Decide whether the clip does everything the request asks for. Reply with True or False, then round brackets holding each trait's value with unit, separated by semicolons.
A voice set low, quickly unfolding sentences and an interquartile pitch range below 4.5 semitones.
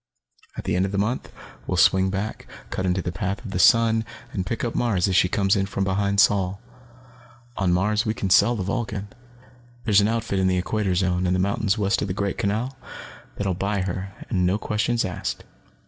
True (100 Hz; 215 wpm; 2.4 semitones)